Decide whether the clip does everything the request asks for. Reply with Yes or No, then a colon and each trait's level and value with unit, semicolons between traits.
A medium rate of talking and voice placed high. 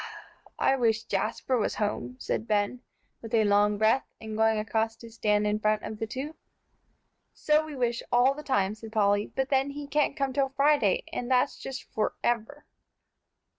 Yes: average, 175 wpm; high, 225 Hz